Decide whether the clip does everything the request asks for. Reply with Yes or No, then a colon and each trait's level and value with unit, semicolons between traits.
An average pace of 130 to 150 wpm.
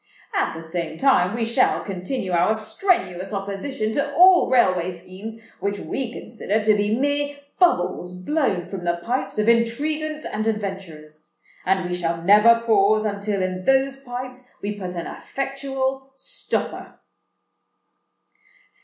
Yes: slow, 135 wpm